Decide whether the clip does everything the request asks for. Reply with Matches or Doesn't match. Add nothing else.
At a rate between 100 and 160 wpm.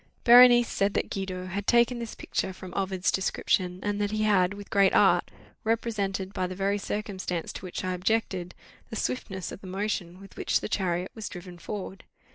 Doesn't match